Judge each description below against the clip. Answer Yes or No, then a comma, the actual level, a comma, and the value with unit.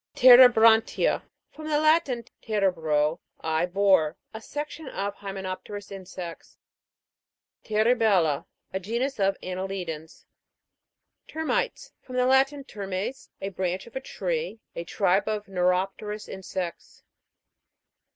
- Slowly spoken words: Yes, slow, 115 wpm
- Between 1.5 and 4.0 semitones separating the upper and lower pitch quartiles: No, average, 5.1 semitones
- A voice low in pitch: No, high, 200 Hz